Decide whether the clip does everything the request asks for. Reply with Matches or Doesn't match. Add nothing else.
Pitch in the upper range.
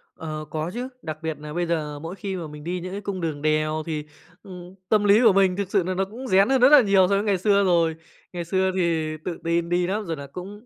Doesn't match